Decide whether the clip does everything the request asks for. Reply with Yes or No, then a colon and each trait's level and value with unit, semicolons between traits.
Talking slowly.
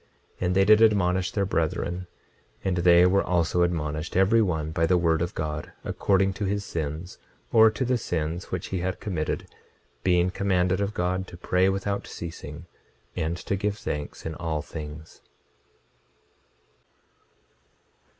No: average, 150 wpm